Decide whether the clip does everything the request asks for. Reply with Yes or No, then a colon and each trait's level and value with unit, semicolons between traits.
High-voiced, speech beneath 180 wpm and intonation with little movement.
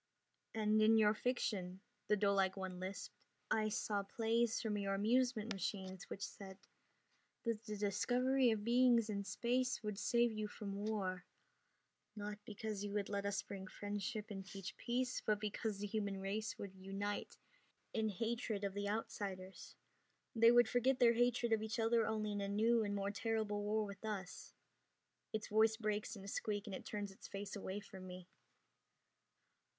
Yes: high, 210 Hz; average, 170 wpm; narrow, 2.1 semitones